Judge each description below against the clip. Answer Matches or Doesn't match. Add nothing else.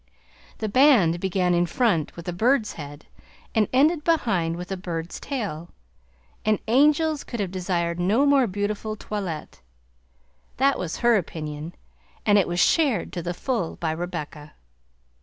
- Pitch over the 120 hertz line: Matches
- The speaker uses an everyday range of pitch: Doesn't match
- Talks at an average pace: Matches